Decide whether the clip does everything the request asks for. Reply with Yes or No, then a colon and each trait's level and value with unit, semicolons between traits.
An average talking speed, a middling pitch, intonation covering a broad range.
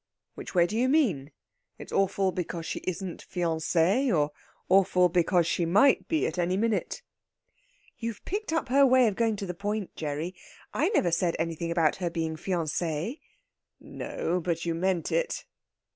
No: average, 165 wpm; medium, 180 Hz; average, 4.5 semitones